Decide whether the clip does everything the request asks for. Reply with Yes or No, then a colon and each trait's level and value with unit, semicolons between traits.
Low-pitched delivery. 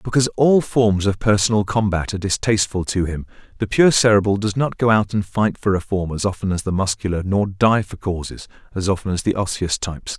Yes: low, 100 Hz